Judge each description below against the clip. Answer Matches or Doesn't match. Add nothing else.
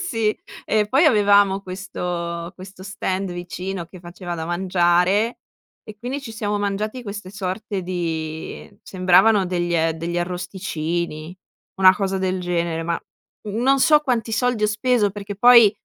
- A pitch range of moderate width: Matches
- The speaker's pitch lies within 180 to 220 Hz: Matches